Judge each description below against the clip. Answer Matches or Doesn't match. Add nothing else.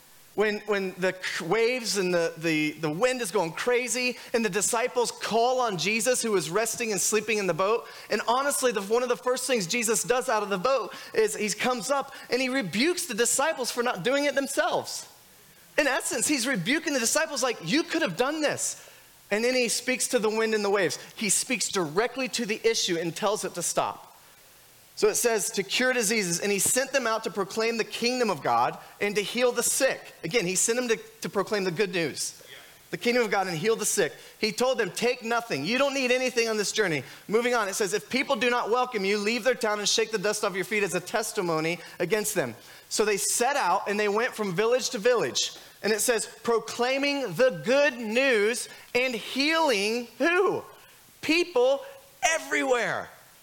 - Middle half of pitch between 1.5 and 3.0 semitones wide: Doesn't match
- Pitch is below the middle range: Doesn't match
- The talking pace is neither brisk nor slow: Doesn't match